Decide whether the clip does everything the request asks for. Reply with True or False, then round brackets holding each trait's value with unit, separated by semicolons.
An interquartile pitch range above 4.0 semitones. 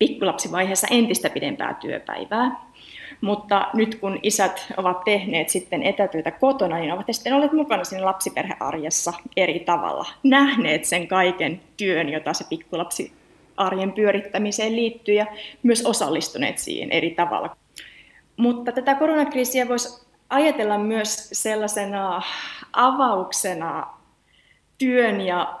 True (4.7 semitones)